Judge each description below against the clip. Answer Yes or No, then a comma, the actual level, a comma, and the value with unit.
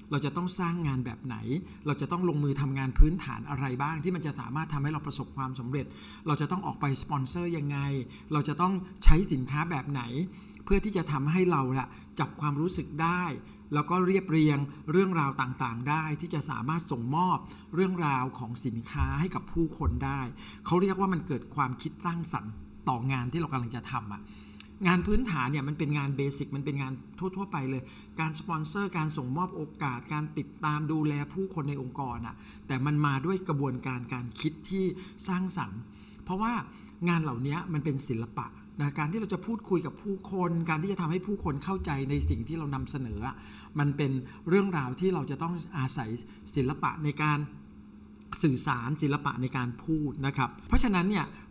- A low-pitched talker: No, medium, 150 Hz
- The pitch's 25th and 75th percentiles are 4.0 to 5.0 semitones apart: Yes, average, 4.6 semitones